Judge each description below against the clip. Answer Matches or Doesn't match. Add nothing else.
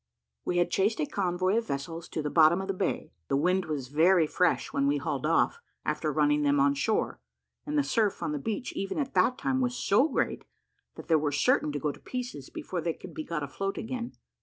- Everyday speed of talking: Doesn't match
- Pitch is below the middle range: Doesn't match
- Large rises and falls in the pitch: Matches